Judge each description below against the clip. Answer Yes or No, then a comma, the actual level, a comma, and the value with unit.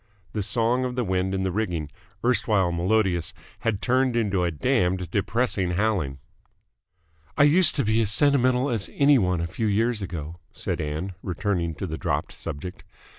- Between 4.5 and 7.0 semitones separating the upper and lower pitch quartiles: Yes, average, 5.2 semitones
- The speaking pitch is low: Yes, low, 100 Hz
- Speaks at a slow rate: No, average, 170 wpm